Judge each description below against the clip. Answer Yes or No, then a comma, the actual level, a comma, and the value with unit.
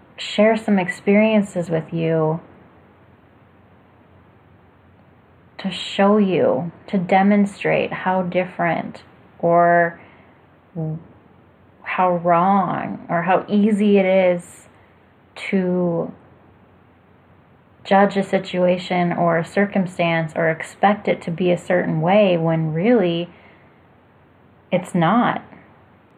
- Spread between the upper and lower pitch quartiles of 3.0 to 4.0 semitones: Yes, average, 3.3 semitones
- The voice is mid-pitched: Yes, medium, 180 Hz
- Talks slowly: Yes, slow, 90 wpm